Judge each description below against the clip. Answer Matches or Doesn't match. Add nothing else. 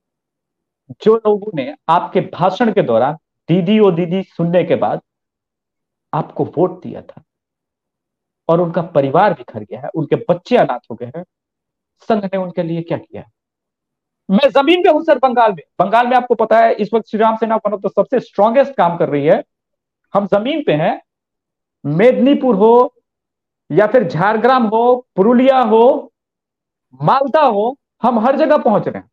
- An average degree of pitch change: Doesn't match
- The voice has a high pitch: Matches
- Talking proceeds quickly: Doesn't match